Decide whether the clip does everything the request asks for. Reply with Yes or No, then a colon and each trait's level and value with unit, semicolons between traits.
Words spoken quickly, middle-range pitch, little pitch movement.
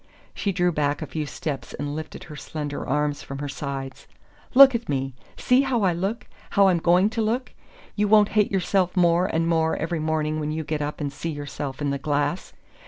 No: fast, 210 wpm; medium, 160 Hz; average, 4.7 semitones